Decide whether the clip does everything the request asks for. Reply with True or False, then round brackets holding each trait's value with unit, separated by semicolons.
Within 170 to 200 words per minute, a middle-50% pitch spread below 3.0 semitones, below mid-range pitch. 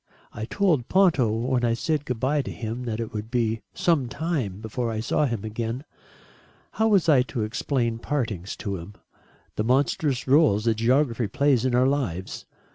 False (180 wpm; 4.1 semitones; 120 Hz)